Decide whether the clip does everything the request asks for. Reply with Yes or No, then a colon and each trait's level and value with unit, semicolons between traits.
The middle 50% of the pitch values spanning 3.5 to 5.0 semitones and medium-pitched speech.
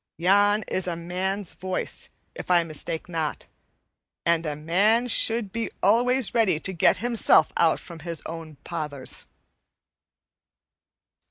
Yes: average, 4.0 semitones; medium, 180 Hz